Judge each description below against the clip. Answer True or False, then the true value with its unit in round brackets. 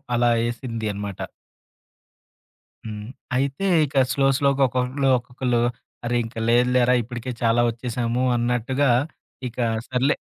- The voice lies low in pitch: True (125 Hz)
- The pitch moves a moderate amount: False (1.8 semitones)